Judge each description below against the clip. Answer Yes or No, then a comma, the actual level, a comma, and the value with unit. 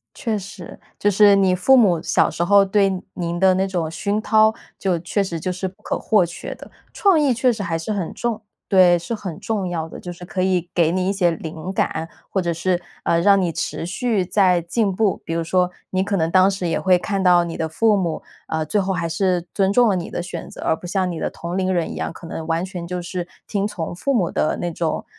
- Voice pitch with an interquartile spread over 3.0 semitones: No, average, 2.7 semitones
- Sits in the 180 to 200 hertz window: Yes, medium, 185 Hz